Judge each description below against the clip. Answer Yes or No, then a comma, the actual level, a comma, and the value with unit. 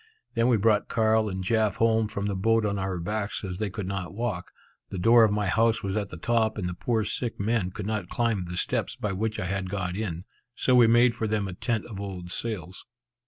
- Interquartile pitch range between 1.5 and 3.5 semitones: Yes, average, 3.1 semitones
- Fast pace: Yes, fast, 235 wpm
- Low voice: Yes, low, 105 Hz